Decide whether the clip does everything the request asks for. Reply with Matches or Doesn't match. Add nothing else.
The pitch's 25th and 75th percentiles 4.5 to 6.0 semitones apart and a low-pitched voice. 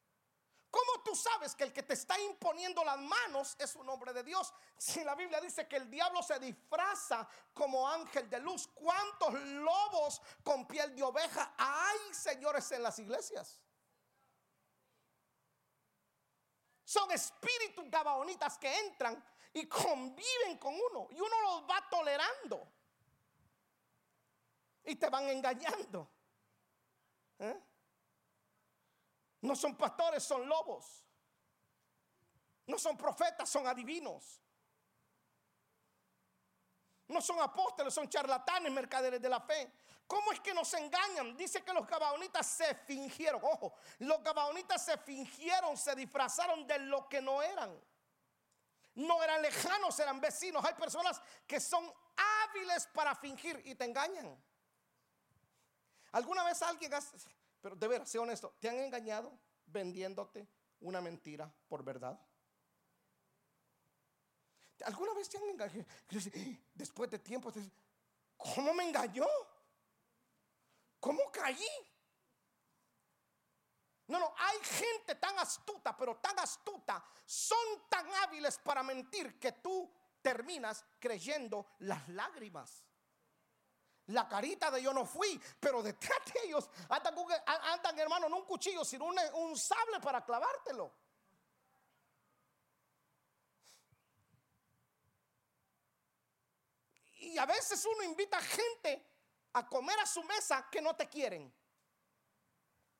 Doesn't match